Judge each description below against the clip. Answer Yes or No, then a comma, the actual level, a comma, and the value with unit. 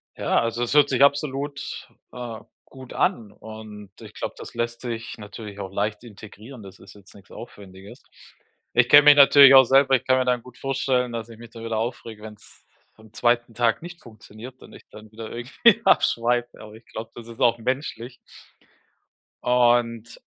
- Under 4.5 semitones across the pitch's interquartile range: Yes, average, 2.9 semitones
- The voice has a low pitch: Yes, low, 120 Hz